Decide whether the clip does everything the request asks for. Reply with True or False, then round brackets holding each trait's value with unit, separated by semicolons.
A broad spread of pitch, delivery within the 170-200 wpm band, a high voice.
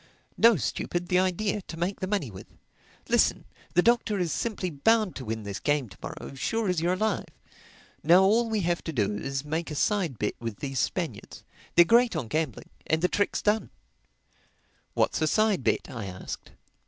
False (7.0 semitones; 180 wpm; 175 Hz)